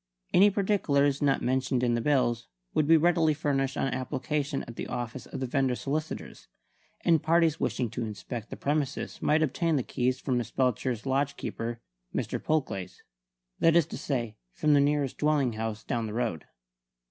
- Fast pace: No, average, 175 wpm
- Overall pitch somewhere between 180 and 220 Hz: No, low, 135 Hz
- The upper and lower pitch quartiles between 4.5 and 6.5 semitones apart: No, average, 3.8 semitones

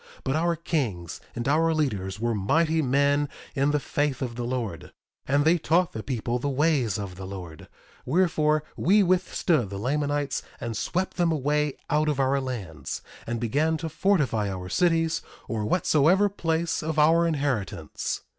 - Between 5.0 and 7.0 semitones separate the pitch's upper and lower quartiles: Yes, wide, 5.5 semitones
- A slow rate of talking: No, average, 165 wpm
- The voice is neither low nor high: Yes, medium, 145 Hz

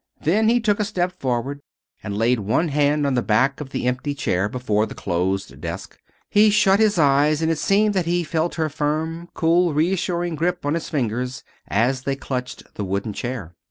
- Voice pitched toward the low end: No, medium, 145 Hz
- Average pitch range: No, wide, 5.7 semitones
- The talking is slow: No, average, 195 wpm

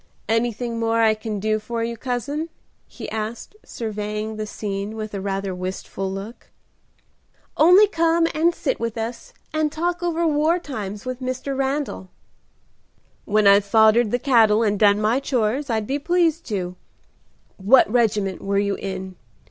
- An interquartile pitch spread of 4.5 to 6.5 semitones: Yes, average, 4.9 semitones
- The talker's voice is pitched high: Yes, high, 225 Hz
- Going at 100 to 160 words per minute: Yes, average, 155 wpm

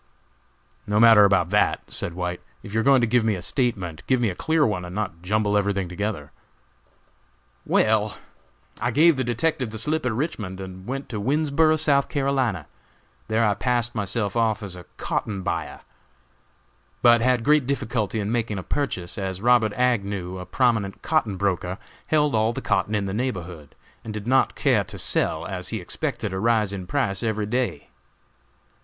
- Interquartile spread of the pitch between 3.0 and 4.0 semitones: No, average, 4.4 semitones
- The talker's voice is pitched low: Yes, low, 110 Hz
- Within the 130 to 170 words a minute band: No, average, 180 wpm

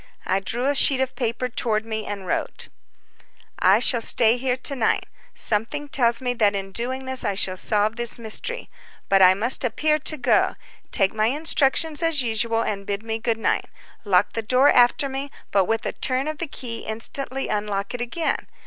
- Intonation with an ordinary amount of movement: Yes, average, 3.7 semitones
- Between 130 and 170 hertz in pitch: No, high, 235 Hz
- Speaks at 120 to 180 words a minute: No, average, 195 wpm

